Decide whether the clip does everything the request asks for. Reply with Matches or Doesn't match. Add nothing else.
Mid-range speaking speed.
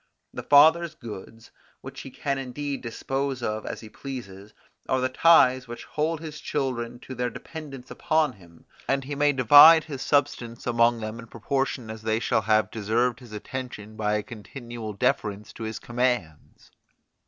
Matches